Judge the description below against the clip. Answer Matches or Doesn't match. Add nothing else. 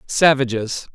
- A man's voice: Matches